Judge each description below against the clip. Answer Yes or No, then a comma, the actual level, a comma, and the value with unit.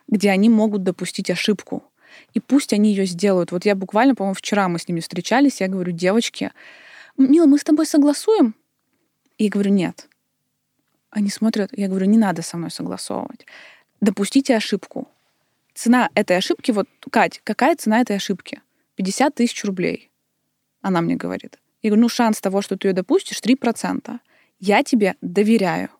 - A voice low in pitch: No, high, 215 Hz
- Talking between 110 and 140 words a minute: No, fast, 160 wpm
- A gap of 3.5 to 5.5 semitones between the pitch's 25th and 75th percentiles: Yes, average, 4.3 semitones